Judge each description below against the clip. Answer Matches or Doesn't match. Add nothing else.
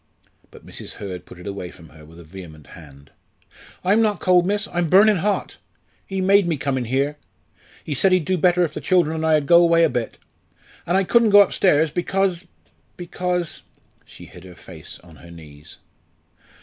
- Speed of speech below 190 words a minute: Doesn't match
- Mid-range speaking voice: Matches